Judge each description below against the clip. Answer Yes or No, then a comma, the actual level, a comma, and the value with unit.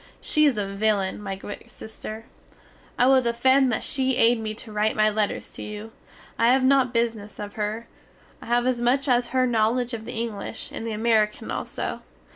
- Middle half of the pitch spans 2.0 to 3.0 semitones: Yes, narrow, 2.6 semitones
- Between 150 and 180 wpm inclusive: No, average, 195 wpm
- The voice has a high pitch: Yes, high, 230 Hz